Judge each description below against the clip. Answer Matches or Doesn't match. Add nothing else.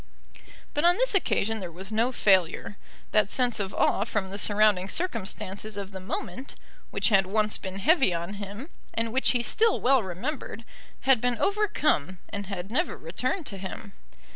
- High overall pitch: Matches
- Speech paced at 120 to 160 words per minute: Doesn't match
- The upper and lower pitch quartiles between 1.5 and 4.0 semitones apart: Doesn't match